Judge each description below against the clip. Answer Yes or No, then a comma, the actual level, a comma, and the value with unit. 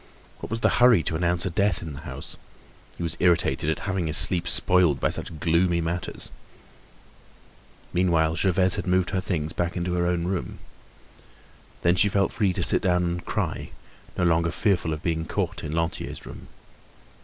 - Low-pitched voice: Yes, very low, 85 Hz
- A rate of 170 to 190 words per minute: Yes, average, 180 wpm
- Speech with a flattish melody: Yes, narrow, 1.8 semitones